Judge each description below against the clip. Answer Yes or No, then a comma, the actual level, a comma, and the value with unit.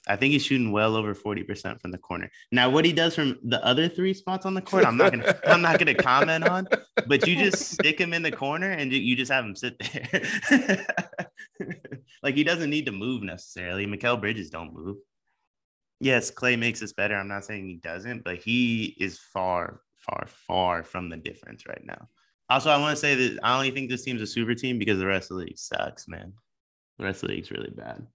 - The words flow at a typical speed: No, fast, 220 wpm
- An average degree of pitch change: No, wide, 6.9 semitones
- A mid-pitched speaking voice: No, low, 125 Hz